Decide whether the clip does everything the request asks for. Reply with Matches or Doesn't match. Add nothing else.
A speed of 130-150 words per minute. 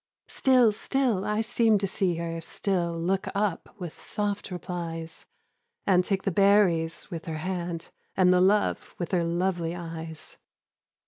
Matches